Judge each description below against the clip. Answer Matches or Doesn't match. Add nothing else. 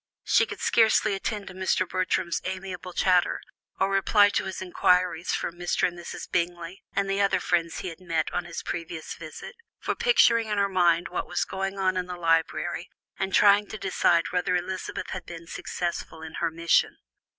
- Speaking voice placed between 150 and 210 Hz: Matches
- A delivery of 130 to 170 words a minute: Doesn't match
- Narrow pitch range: Matches